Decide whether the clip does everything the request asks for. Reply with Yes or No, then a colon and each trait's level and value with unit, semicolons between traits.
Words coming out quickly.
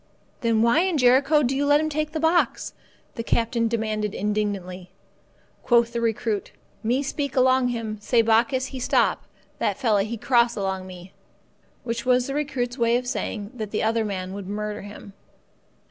No: average, 170 wpm